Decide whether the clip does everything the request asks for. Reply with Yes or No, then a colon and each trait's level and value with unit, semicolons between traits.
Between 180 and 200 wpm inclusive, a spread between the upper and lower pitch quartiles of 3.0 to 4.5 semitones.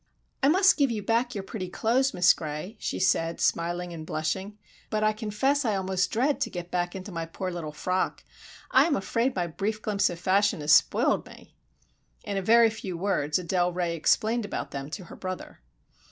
Yes: average, 195 wpm; average, 4.0 semitones